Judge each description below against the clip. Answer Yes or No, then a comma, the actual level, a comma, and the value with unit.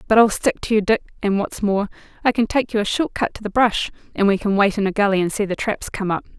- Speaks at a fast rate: Yes, fast, 300 wpm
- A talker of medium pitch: No, high, 210 Hz